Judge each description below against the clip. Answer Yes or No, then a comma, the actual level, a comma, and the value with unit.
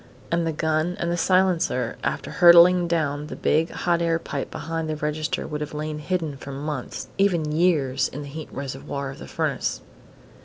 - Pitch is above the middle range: No, medium, 155 Hz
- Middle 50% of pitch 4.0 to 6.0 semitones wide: No, average, 2.8 semitones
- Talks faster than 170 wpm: Yes, average, 180 wpm